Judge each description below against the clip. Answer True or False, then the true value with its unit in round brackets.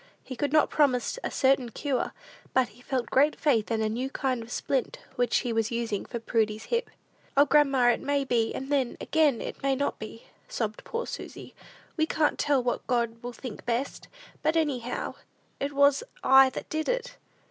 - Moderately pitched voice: False (260 Hz)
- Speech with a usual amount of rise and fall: True (3.3 semitones)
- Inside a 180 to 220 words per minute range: True (190 wpm)